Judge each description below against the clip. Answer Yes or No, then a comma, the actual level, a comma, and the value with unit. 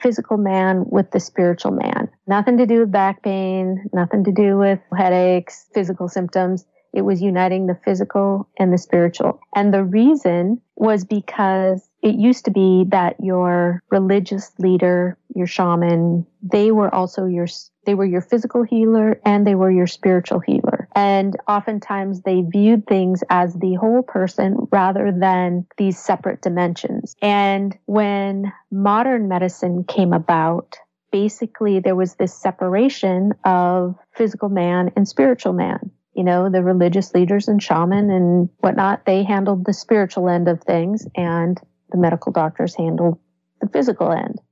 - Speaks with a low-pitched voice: No, high, 190 Hz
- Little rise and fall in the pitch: Yes, narrow, 2.3 semitones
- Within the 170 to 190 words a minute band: No, average, 150 wpm